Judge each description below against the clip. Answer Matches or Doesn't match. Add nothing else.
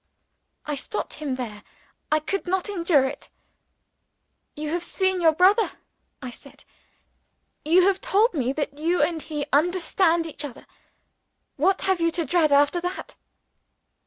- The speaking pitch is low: Doesn't match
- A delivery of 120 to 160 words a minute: Matches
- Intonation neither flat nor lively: Matches